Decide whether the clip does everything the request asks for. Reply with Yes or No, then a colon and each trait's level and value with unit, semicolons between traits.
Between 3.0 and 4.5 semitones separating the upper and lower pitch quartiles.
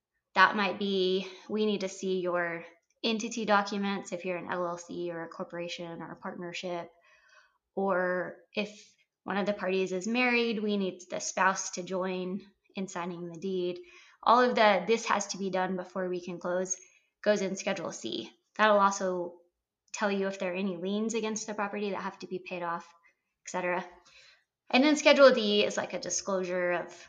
No: narrow, 2.5 semitones